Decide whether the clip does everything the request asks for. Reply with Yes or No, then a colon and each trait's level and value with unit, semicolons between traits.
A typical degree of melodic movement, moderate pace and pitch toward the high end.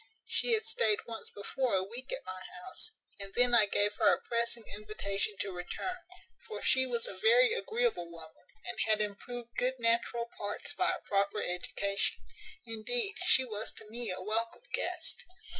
Yes: average, 4.3 semitones; average, 175 wpm; high, 230 Hz